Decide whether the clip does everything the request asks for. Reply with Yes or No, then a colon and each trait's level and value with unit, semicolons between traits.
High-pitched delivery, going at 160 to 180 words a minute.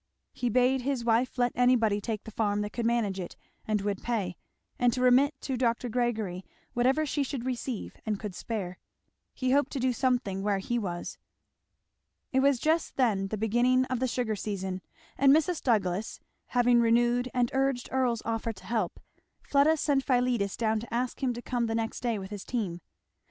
No: high, 240 Hz; average, 190 wpm